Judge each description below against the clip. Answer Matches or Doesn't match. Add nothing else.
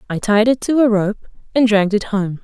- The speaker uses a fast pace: Matches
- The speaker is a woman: Matches